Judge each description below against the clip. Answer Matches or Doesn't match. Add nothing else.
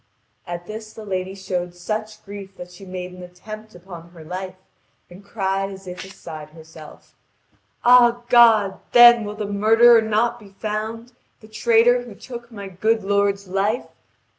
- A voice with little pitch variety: Doesn't match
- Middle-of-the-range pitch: Doesn't match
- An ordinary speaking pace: Matches